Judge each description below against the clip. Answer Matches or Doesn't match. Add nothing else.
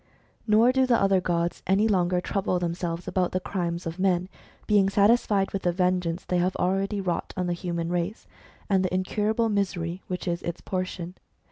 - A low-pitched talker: Doesn't match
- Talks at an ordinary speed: Matches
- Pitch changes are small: Matches